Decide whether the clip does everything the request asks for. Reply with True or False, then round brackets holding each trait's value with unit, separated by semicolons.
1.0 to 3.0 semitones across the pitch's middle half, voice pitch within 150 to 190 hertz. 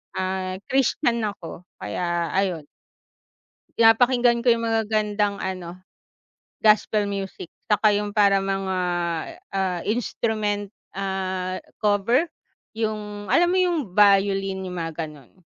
False (2.7 semitones; 200 Hz)